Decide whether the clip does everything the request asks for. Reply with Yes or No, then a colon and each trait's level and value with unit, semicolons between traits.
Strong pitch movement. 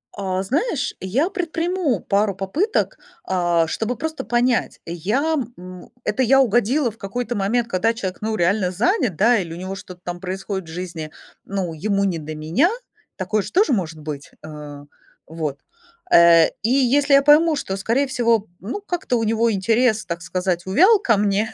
Yes: wide, 5.9 semitones